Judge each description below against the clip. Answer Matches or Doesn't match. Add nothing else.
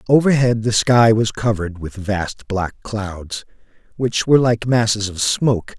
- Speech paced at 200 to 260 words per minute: Doesn't match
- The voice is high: Doesn't match